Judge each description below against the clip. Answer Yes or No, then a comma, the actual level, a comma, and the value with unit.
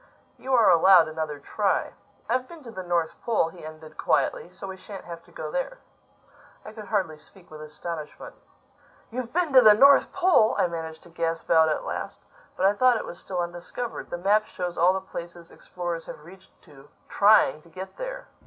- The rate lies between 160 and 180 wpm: No, average, 200 wpm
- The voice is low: No, medium, 185 Hz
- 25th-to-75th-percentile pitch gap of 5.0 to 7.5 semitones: Yes, average, 5.3 semitones